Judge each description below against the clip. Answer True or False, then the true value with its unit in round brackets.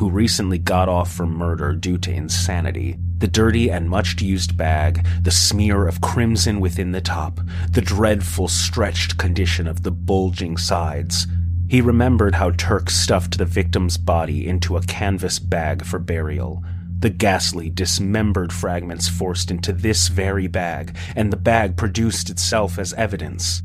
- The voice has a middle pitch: False (90 Hz)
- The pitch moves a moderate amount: False (1.8 semitones)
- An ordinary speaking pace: True (150 wpm)